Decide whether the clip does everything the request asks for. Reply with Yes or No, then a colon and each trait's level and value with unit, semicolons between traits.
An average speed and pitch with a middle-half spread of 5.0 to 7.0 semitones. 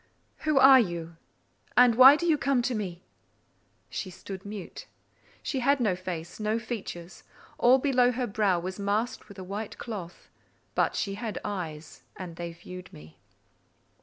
Yes: average, 155 wpm; wide, 5.5 semitones